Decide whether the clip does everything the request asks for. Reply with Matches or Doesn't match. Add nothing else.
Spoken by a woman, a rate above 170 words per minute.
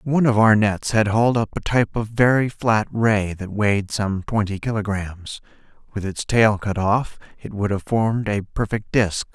Doesn't match